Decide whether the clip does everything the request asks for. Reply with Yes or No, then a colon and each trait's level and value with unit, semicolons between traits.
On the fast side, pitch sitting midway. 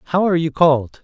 Yes: fast, 230 wpm; medium, 155 Hz